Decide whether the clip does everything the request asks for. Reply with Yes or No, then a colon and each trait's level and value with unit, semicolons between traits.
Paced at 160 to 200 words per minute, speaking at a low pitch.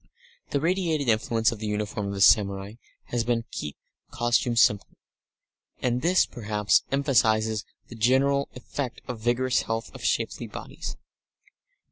No: average, 140 wpm; low, 115 Hz